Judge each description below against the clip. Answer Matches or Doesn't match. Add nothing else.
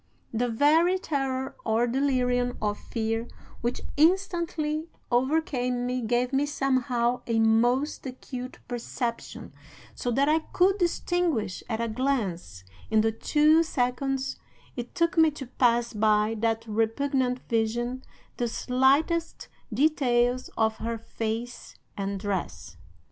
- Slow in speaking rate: Matches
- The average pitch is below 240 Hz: Doesn't match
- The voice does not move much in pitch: Doesn't match